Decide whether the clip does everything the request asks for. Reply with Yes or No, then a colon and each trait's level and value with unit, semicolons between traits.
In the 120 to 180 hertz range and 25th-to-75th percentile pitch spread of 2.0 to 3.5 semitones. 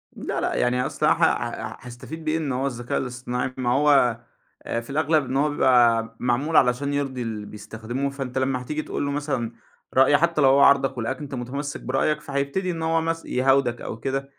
Yes: low, 135 Hz; average, 2.7 semitones